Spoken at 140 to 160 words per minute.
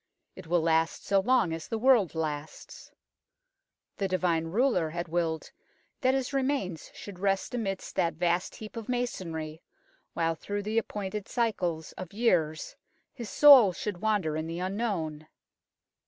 Yes: average, 150 wpm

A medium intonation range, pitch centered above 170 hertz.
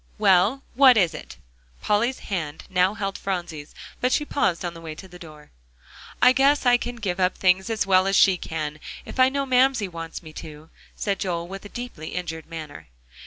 No: wide, 6.0 semitones; high, 190 Hz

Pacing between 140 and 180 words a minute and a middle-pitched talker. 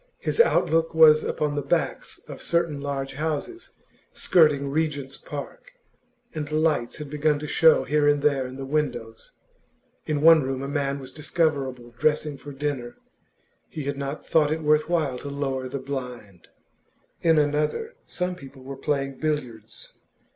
Yes: average, 155 wpm; medium, 145 Hz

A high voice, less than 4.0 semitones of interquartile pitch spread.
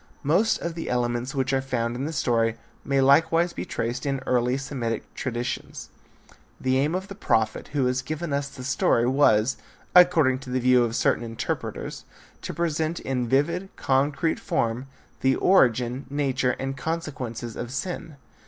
No: low, 135 Hz; average, 3.6 semitones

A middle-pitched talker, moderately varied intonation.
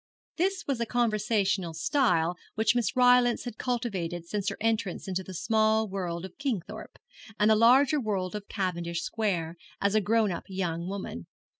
No: high, 210 Hz; average, 4.2 semitones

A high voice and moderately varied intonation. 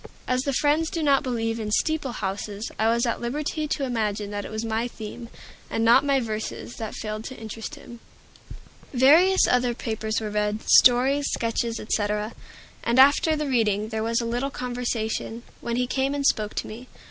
Yes: high, 235 Hz; average, 3.4 semitones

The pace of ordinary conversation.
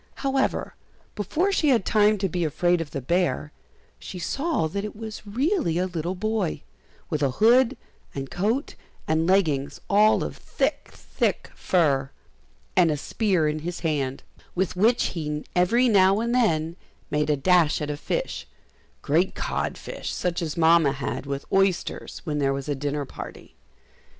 Yes: average, 165 wpm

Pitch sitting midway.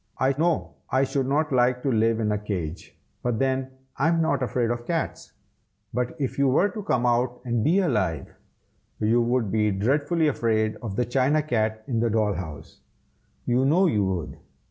No: low, 125 Hz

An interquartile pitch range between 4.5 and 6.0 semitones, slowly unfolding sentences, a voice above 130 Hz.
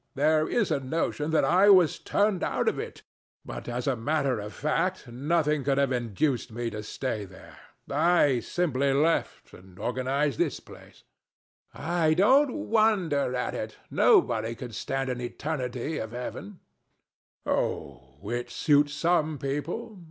No: average, 5.2 semitones; average, 160 wpm; medium, 140 Hz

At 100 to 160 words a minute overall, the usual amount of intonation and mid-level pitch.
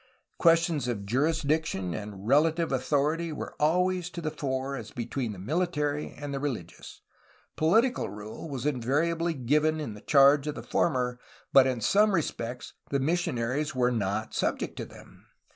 Yes: average, 150 wpm; average, 4.7 semitones; medium, 145 Hz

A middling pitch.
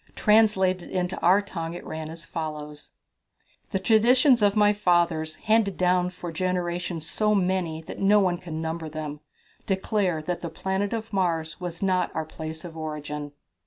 Yes: medium, 180 Hz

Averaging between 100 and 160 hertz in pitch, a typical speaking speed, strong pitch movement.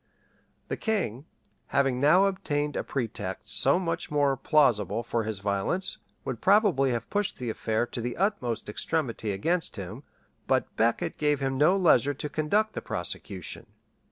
Yes: medium, 140 Hz; average, 155 wpm; wide, 6.5 semitones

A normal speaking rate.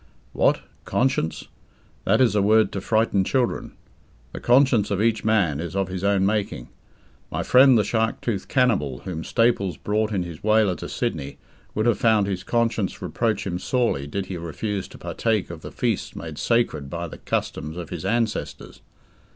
Yes: average, 175 wpm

